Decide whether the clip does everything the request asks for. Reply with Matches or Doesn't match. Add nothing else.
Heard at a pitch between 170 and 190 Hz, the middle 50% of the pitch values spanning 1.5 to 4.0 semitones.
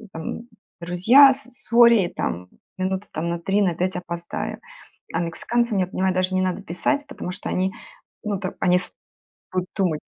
Matches